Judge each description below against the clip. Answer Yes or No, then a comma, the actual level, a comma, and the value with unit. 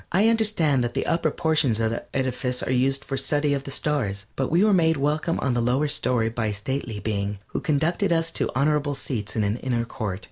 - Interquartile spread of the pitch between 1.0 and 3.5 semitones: No, average, 4.6 semitones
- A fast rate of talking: Yes, fast, 225 wpm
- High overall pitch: No, low, 135 Hz